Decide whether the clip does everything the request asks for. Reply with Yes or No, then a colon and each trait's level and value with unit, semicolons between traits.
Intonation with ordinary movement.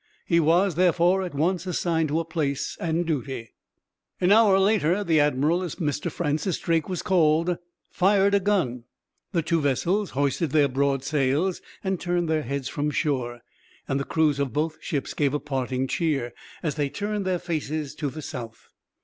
Yes: average, 4.0 semitones